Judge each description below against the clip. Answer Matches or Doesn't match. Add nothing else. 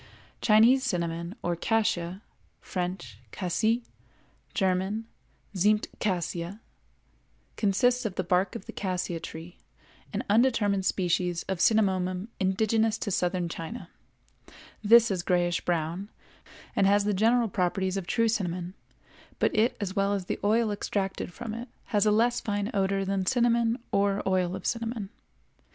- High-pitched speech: Matches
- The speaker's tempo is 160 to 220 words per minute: Doesn't match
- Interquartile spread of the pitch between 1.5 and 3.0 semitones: Doesn't match